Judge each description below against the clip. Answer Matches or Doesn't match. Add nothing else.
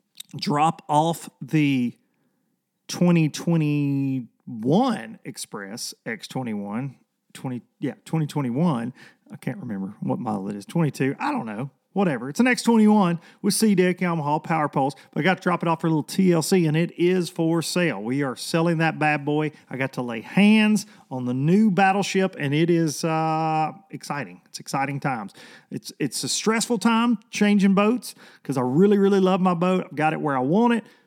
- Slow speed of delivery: Doesn't match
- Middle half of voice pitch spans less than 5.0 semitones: Doesn't match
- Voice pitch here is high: Doesn't match